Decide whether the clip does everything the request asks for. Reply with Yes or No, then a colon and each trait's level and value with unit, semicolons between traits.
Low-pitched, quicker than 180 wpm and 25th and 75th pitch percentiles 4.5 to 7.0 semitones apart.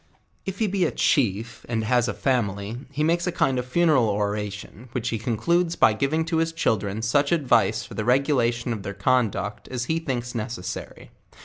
Yes: low, 120 Hz; average, 195 wpm; average, 5.3 semitones